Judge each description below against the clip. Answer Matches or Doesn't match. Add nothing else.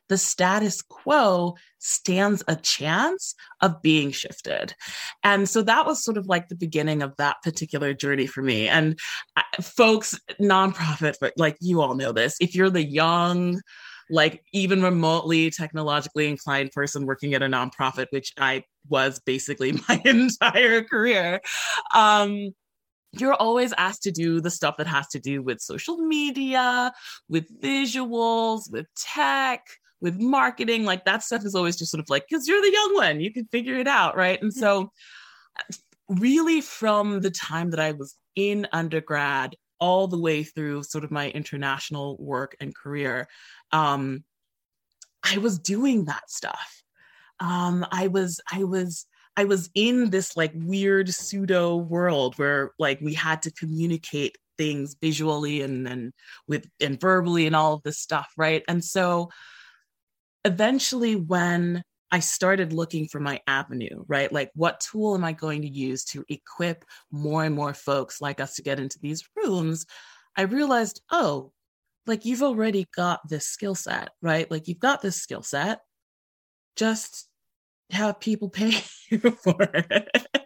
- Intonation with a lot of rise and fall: Matches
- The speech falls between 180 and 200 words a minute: Doesn't match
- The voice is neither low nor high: Matches